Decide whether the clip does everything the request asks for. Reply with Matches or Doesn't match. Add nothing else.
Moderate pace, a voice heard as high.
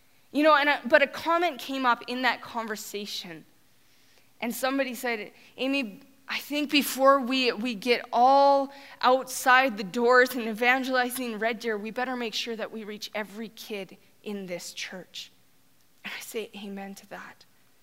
Matches